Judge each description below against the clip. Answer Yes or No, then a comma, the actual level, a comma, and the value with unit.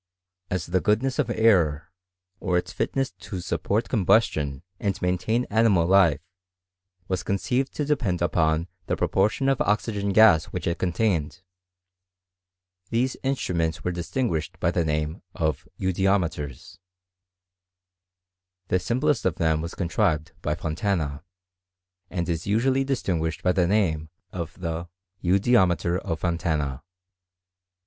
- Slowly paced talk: Yes, slow, 125 wpm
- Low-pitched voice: Yes, very low, 90 Hz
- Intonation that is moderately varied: Yes, average, 4.6 semitones